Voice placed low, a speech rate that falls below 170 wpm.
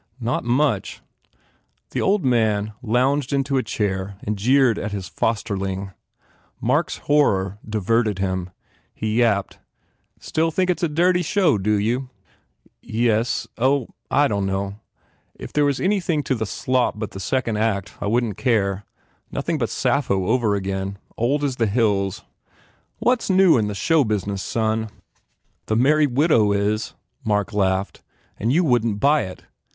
Yes: low, 115 Hz; average, 155 wpm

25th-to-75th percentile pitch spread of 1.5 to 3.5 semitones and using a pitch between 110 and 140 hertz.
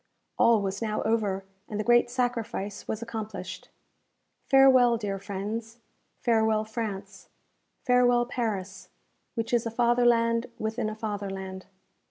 No: average, 2.8 semitones; high, 220 Hz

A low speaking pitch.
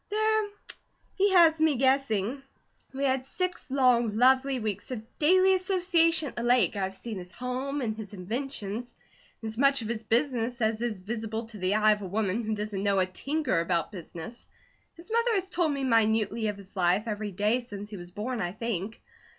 No: high, 230 Hz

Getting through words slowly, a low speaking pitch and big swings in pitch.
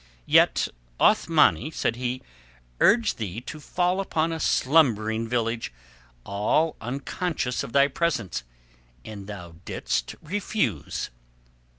Yes: slow, 105 wpm; low, 125 Hz; wide, 6.9 semitones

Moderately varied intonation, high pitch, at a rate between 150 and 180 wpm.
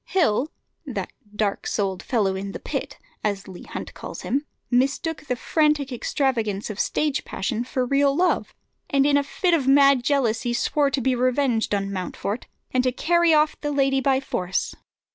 Yes: average, 4.6 semitones; very high, 265 Hz; average, 175 wpm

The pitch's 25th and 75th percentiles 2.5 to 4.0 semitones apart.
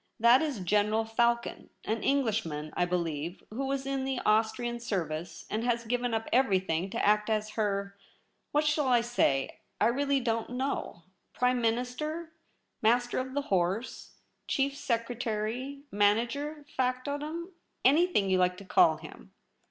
No: average, 4.4 semitones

